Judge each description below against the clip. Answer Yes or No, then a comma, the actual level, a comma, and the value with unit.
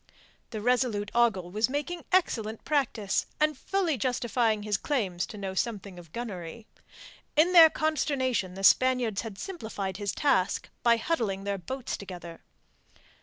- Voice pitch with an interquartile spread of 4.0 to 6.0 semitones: Yes, average, 5.3 semitones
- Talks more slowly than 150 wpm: Yes, average, 140 wpm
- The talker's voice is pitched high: Yes, high, 225 Hz